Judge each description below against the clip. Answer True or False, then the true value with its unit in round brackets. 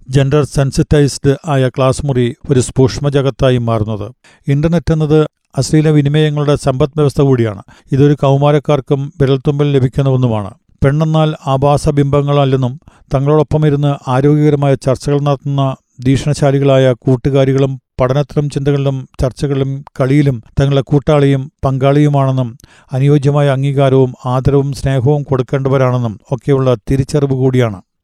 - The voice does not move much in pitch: True (1.6 semitones)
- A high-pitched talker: False (140 Hz)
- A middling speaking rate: True (90 wpm)